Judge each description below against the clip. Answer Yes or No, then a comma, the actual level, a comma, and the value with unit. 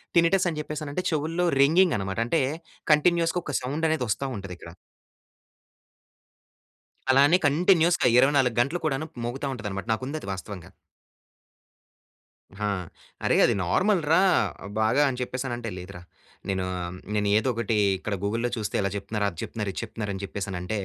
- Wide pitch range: Yes, wide, 7.2 semitones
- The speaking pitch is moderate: No, low, 125 Hz